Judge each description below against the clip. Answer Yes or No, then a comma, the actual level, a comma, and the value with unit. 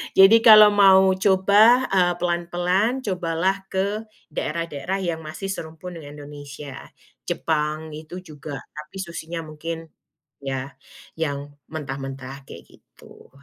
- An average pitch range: Yes, average, 4.4 semitones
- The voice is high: No, medium, 165 Hz